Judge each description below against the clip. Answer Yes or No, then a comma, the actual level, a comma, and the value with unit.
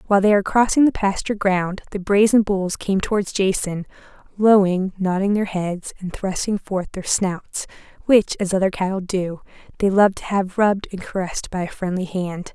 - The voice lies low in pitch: No, high, 195 Hz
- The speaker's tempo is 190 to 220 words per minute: No, average, 180 wpm